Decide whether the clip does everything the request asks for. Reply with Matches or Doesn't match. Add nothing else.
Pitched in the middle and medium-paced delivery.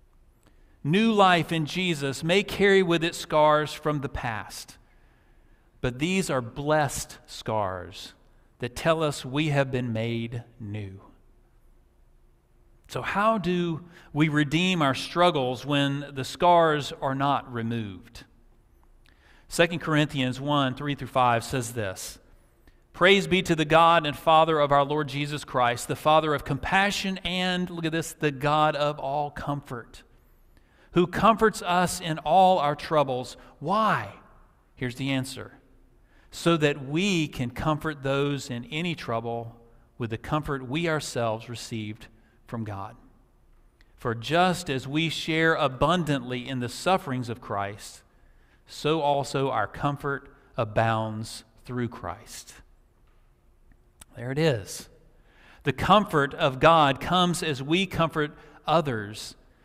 Doesn't match